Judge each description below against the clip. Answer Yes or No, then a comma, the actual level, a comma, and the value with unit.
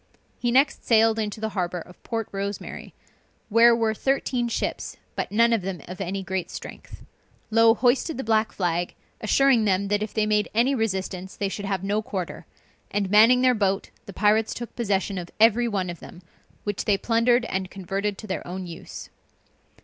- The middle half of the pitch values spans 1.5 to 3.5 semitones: Yes, average, 3.1 semitones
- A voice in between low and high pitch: No, high, 210 Hz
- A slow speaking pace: No, average, 185 wpm